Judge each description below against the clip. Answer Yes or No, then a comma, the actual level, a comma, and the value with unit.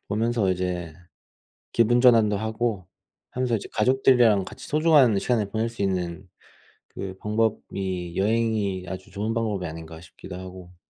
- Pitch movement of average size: Yes, average, 3.8 semitones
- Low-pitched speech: Yes, low, 105 Hz